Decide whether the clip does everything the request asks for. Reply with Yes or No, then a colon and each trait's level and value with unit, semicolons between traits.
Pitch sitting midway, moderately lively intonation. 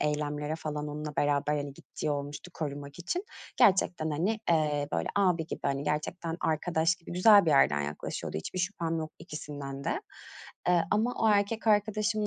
Yes: medium, 155 Hz; average, 3.9 semitones